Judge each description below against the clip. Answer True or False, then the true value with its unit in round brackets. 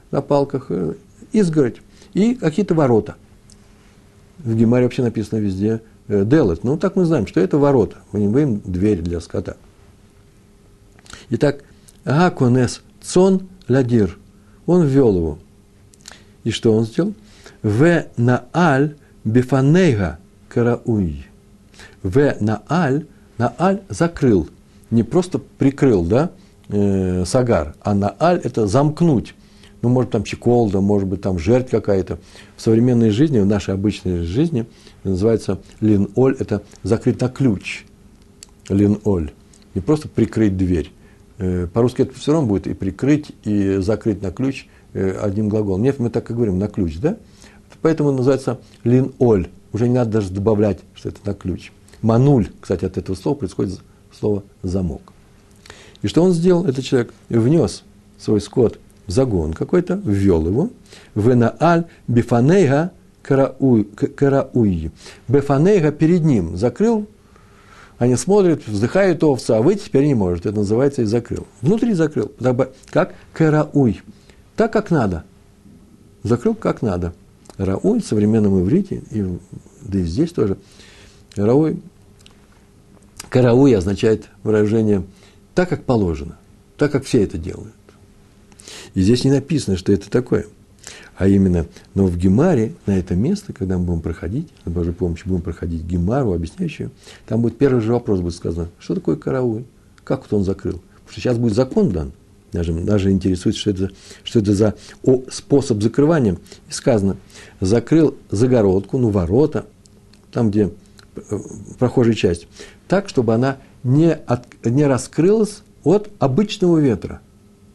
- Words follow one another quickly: False (140 wpm)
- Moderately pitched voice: False (110 Hz)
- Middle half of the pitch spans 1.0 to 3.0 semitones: False (5.1 semitones)